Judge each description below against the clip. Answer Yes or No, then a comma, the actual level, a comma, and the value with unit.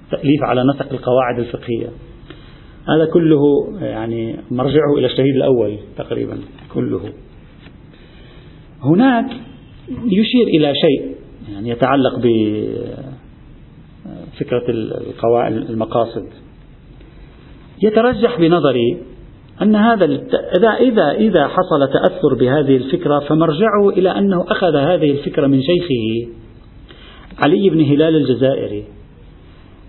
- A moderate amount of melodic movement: No, wide, 5.9 semitones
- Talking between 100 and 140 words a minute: No, average, 90 wpm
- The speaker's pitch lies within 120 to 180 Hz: Yes, medium, 140 Hz